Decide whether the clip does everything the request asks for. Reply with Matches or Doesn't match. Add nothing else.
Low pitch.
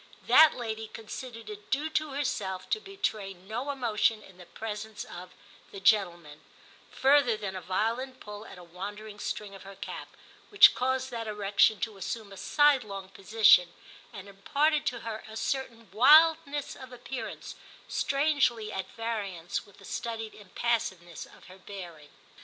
Doesn't match